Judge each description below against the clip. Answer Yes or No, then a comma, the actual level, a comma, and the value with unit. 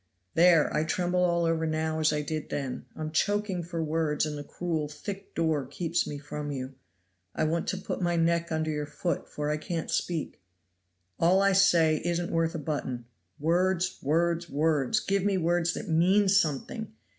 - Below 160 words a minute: No, average, 180 wpm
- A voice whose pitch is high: No, medium, 165 Hz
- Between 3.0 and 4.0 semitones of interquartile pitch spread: No, narrow, 2.5 semitones